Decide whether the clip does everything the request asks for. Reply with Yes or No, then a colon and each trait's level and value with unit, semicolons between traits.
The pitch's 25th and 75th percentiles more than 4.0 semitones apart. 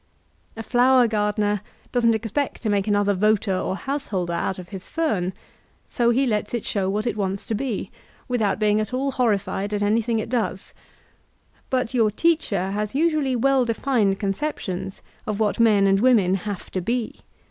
No: average, 3.7 semitones